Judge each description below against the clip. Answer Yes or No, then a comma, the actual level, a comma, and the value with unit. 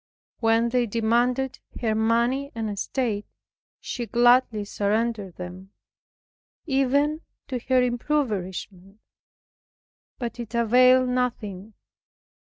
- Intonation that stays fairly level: No, average, 3.1 semitones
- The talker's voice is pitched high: Yes, high, 235 Hz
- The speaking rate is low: Yes, slow, 90 wpm